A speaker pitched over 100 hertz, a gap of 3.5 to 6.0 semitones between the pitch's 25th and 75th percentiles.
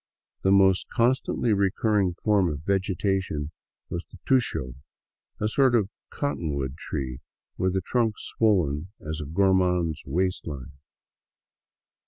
No: very low, 95 Hz; average, 5.1 semitones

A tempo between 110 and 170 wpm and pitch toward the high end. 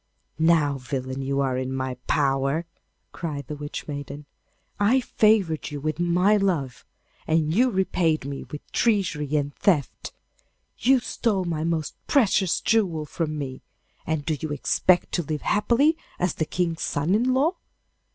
No: average, 150 wpm; medium, 160 Hz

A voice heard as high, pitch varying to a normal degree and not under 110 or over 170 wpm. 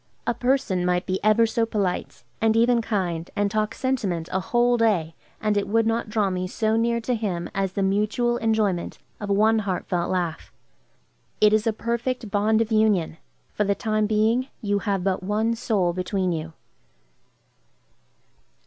Yes: high, 210 Hz; average, 3.2 semitones; average, 165 wpm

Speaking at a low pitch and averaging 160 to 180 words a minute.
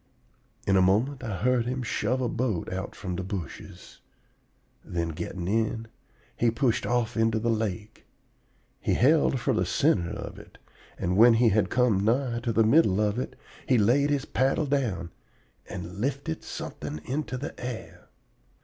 Yes: low, 115 Hz; average, 165 wpm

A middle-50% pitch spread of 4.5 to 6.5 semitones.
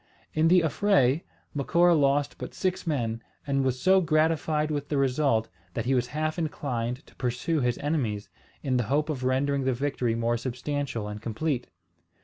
No: average, 3.9 semitones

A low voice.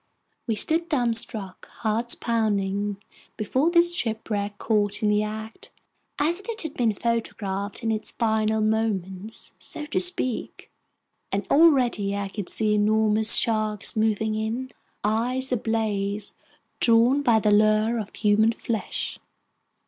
No: high, 220 Hz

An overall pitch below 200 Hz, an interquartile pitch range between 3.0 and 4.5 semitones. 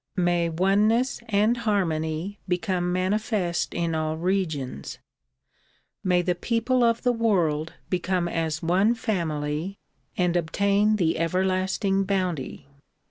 Yes: medium, 185 Hz; average, 3.5 semitones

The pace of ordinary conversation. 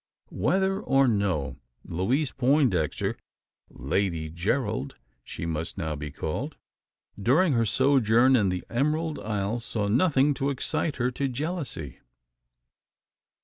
No: slow, 115 wpm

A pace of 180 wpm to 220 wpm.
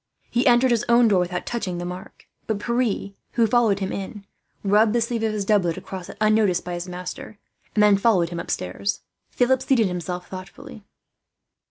Yes: average, 185 wpm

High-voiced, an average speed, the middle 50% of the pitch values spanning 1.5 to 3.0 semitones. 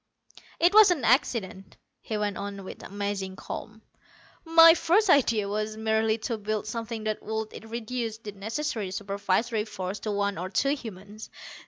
Yes: high, 215 Hz; average, 155 wpm; narrow, 2.5 semitones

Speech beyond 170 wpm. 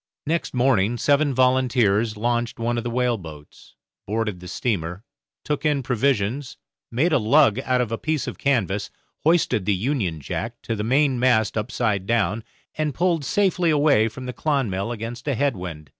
No: average, 165 wpm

